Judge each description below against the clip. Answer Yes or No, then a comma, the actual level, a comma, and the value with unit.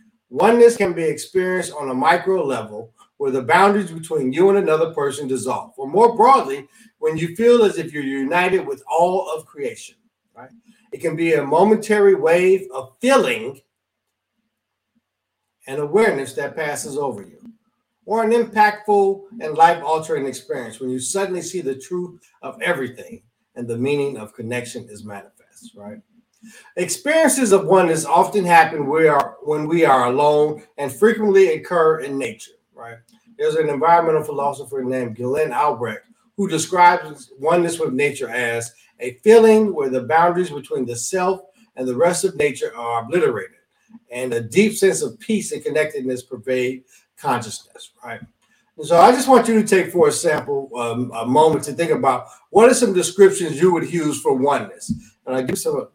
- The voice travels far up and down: Yes, wide, 7.6 semitones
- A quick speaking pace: No, average, 165 wpm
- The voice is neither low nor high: Yes, medium, 175 Hz